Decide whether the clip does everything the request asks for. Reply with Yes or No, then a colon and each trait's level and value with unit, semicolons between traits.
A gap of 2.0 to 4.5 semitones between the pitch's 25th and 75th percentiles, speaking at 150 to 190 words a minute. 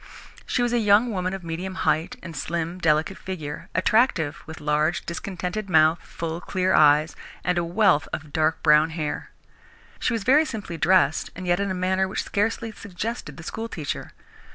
Yes: average, 4.0 semitones; average, 175 wpm